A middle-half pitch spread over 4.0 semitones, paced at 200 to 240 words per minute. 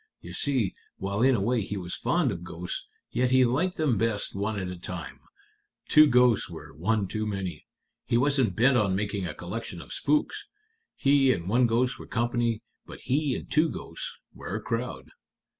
No: average, 4.9 semitones; average, 190 wpm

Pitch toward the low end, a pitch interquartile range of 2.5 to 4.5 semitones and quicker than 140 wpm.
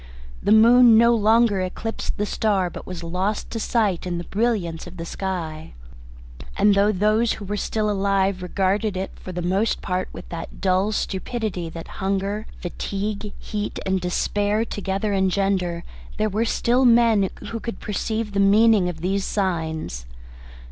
No: high, 200 Hz; average, 2.9 semitones; average, 155 wpm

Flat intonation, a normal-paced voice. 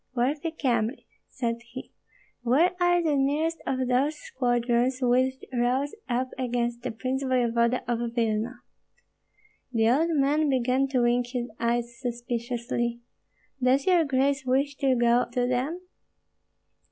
No: narrow, 2.3 semitones; slow, 130 wpm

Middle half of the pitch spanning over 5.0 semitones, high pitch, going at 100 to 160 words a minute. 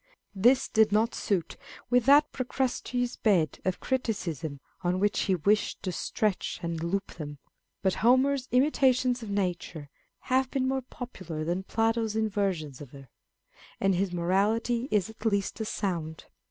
Yes: wide, 5.6 semitones; high, 205 Hz; average, 155 wpm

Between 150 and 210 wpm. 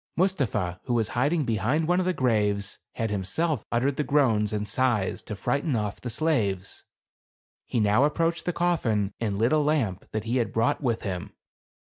Yes: average, 185 wpm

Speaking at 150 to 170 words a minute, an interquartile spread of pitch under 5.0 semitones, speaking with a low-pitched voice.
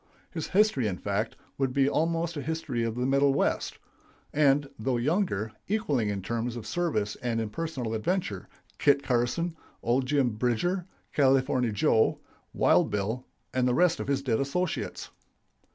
No: average, 155 wpm; wide, 5.5 semitones; low, 130 Hz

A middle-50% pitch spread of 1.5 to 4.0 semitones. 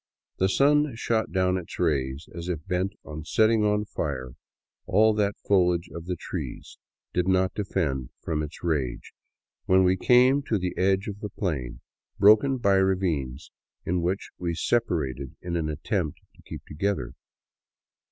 No: average, 4.7 semitones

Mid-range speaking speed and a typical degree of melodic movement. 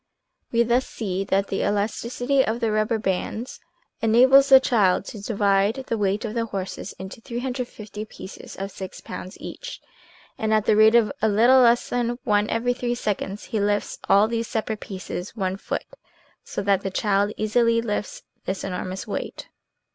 Yes: average, 170 wpm; average, 3.0 semitones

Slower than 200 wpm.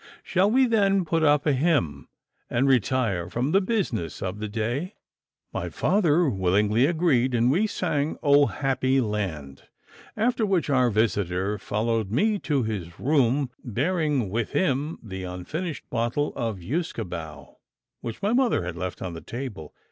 Yes: average, 150 wpm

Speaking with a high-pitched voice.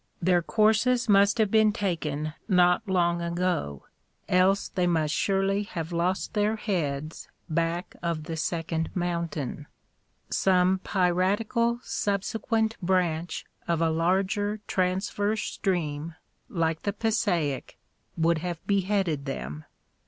No: medium, 180 Hz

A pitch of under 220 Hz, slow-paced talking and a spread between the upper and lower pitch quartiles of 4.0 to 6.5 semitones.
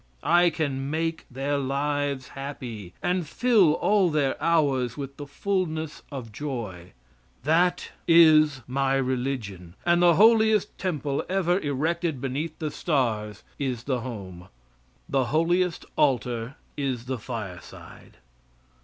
Yes: medium, 140 Hz; slow, 120 wpm; average, 4.6 semitones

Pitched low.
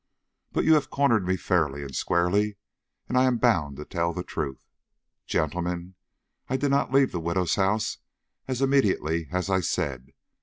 Yes: very low, 90 Hz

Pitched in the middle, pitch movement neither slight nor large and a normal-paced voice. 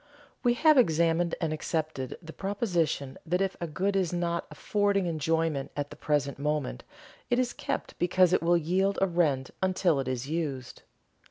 Yes: medium, 170 Hz; average, 3.9 semitones; average, 170 wpm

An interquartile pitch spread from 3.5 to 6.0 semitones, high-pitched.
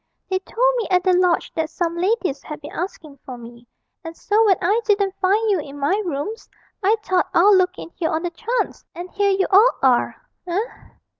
Yes: average, 4.1 semitones; very high, 370 Hz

